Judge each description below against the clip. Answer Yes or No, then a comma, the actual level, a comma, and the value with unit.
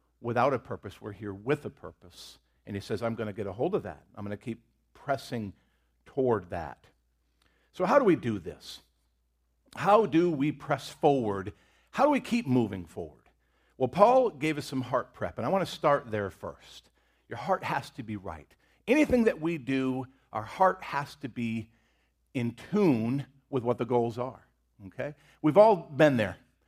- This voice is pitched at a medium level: No, low, 125 Hz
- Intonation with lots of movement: Yes, wide, 6.4 semitones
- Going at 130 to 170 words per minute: No, average, 190 wpm